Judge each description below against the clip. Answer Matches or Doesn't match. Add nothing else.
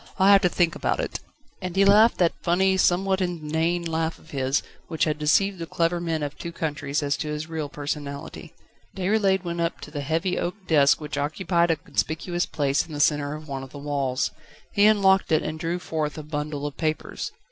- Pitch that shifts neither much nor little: Matches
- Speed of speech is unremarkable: Doesn't match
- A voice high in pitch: Doesn't match